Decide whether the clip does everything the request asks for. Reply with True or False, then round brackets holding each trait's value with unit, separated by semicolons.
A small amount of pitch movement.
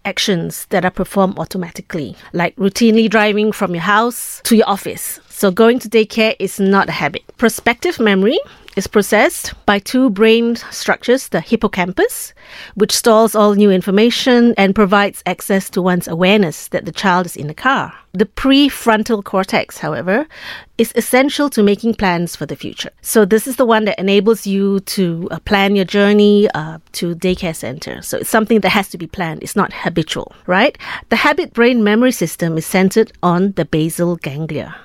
False (3.7 semitones)